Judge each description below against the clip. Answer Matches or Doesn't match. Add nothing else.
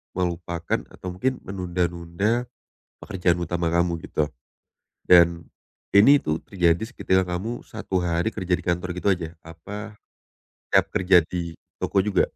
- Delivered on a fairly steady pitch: Matches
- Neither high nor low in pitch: Doesn't match